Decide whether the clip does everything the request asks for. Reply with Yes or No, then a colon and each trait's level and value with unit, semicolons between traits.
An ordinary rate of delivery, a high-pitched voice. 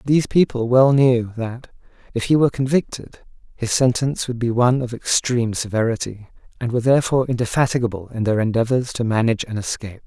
No: average, 165 wpm; low, 120 Hz